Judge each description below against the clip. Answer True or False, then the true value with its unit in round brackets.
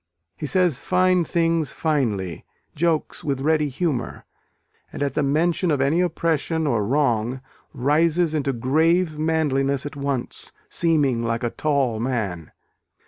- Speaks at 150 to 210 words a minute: False (135 wpm)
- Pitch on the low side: False (145 Hz)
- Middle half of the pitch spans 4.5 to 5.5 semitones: False (4.0 semitones)